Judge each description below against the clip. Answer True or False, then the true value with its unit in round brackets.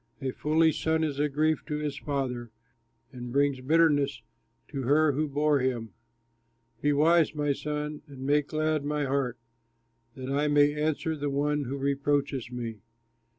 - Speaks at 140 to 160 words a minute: True (155 wpm)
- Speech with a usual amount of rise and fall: False (1.7 semitones)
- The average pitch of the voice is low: False (145 Hz)